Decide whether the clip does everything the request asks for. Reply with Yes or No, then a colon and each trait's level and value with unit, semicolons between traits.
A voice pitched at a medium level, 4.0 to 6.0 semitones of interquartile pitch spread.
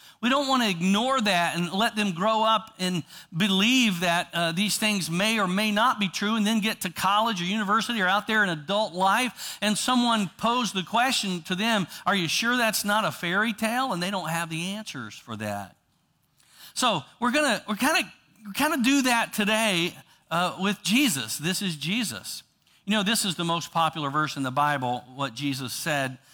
No: high, 200 Hz; average, 4.5 semitones